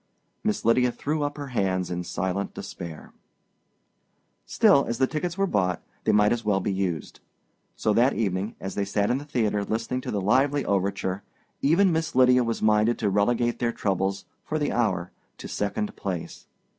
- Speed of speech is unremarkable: Yes, average, 180 wpm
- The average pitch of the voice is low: Yes, low, 110 Hz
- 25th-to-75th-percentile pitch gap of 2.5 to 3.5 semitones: No, average, 5.1 semitones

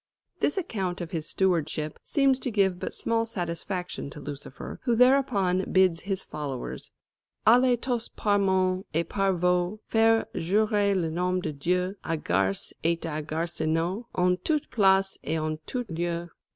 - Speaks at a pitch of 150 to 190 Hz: Yes, medium, 185 Hz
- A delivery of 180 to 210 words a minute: No, average, 155 wpm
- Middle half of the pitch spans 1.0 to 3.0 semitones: No, average, 4.3 semitones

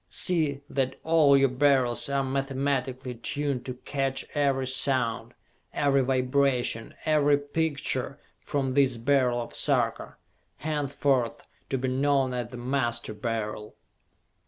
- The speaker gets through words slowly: Yes, slow, 120 wpm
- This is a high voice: No, low, 135 Hz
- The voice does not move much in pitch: Yes, narrow, 2.1 semitones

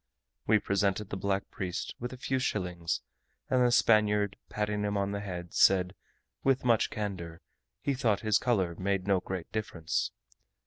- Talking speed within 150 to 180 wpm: Yes, average, 165 wpm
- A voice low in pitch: Yes, low, 100 Hz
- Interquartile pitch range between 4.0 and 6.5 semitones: No, narrow, 2.6 semitones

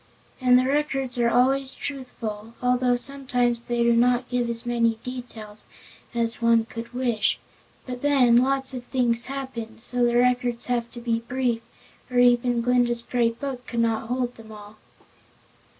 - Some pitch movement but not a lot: No, narrow, 1.3 semitones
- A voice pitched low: No, high, 245 Hz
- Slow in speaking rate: No, average, 165 wpm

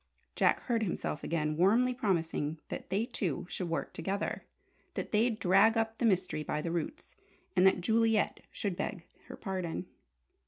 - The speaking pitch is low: No, high, 190 Hz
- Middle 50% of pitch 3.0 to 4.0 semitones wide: No, average, 4.8 semitones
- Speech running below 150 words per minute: No, average, 160 wpm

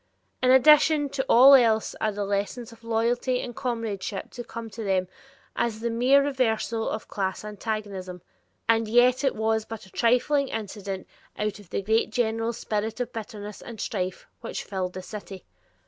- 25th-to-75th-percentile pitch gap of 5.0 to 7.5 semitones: No, average, 2.9 semitones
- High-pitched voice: Yes, high, 225 Hz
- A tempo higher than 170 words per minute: No, average, 165 wpm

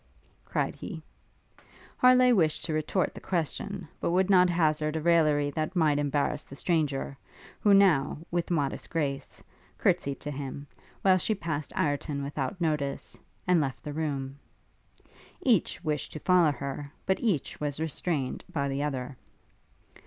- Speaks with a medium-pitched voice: Yes, medium, 155 Hz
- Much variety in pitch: No, average, 3.7 semitones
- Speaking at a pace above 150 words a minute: No, average, 145 wpm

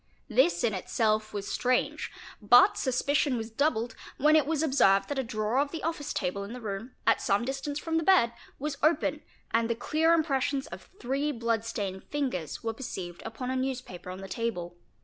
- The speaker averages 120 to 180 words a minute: No, average, 190 wpm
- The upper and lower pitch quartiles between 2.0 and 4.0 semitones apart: No, average, 4.9 semitones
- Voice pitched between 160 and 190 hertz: No, high, 245 Hz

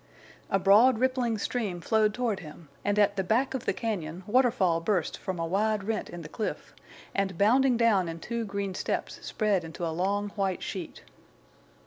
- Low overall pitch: No, high, 200 Hz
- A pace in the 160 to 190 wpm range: Yes, average, 180 wpm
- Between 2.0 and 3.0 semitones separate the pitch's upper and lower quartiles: No, average, 3.7 semitones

